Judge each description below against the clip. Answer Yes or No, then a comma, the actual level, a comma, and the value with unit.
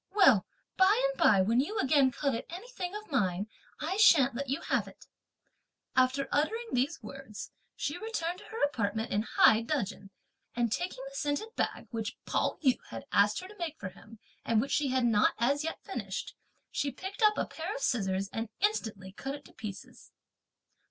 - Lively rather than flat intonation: Yes, wide, 8.4 semitones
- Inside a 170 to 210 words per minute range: Yes, average, 185 wpm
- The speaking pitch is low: No, very high, 275 Hz